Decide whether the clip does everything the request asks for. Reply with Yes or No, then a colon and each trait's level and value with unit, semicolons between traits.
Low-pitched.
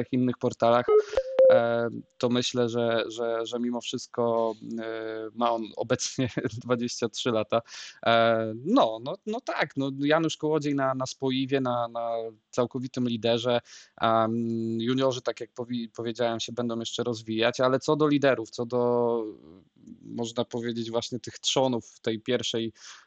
Yes: low, 120 Hz